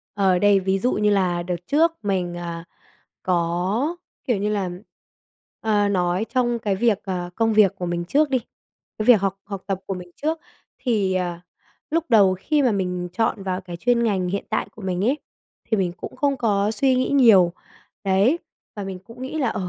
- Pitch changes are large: No, average, 4.2 semitones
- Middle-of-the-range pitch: No, high, 200 Hz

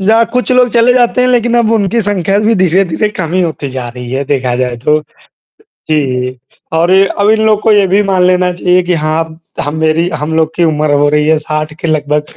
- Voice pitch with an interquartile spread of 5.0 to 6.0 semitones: Yes, wide, 5.5 semitones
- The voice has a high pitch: No, medium, 175 Hz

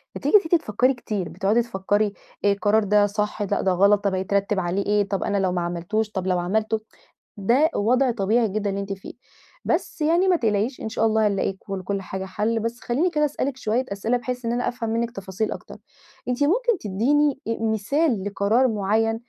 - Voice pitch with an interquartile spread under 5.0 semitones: Yes, average, 3.5 semitones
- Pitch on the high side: Yes, high, 215 Hz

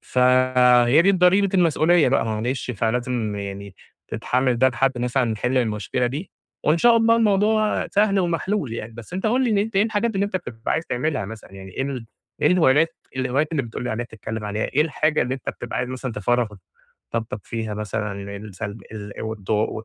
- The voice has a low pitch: Yes, low, 125 Hz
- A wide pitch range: Yes, wide, 7.0 semitones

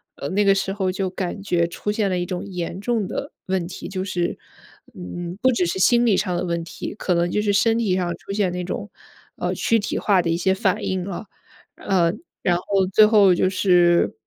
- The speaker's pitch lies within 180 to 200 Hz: Yes, high, 190 Hz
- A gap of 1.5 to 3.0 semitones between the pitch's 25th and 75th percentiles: Yes, narrow, 2.4 semitones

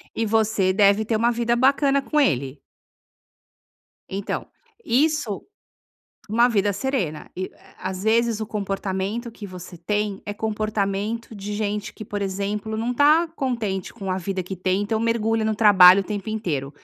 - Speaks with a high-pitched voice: Yes, high, 210 Hz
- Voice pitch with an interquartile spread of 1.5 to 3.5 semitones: Yes, average, 2.9 semitones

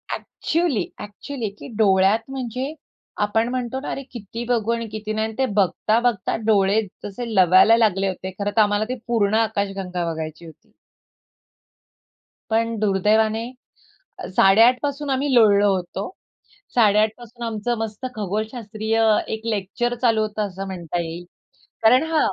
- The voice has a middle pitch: No, high, 220 Hz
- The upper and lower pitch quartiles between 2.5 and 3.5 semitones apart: Yes, average, 2.9 semitones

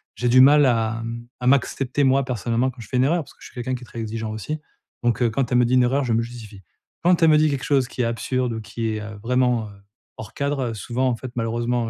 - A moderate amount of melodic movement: No, narrow, 2.3 semitones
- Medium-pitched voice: No, low, 120 Hz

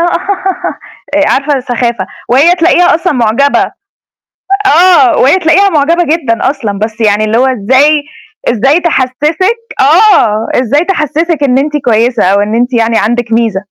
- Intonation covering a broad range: Yes, wide, 6.3 semitones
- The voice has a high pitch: Yes, very high, 275 Hz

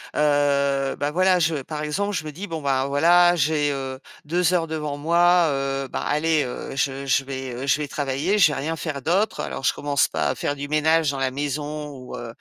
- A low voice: No, medium, 145 Hz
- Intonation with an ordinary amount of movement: Yes, average, 3.0 semitones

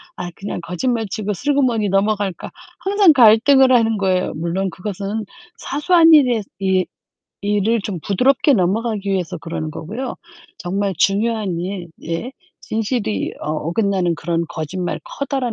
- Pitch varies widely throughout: No, average, 4.5 semitones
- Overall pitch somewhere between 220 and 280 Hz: No, high, 205 Hz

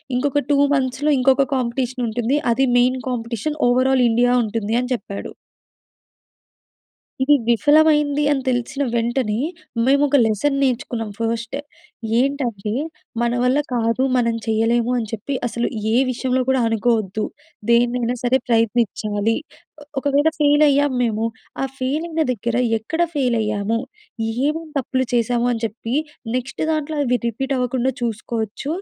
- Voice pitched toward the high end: Yes, high, 245 Hz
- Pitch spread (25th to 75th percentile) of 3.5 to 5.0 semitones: No, average, 2.9 semitones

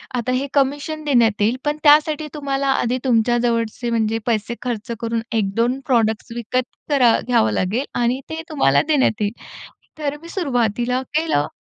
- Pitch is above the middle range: Yes, high, 245 Hz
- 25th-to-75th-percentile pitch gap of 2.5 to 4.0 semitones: Yes, average, 3.7 semitones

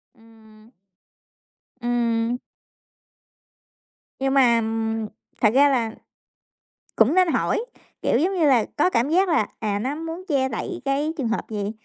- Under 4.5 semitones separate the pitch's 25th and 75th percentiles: No, average, 4.8 semitones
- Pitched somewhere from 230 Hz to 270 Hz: Yes, very high, 250 Hz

